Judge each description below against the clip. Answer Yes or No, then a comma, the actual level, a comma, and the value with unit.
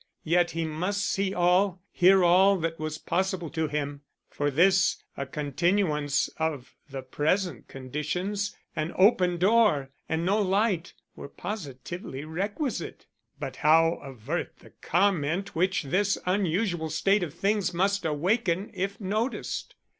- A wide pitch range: No, average, 4.2 semitones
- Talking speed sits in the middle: No, slow, 130 wpm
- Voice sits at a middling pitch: Yes, medium, 175 Hz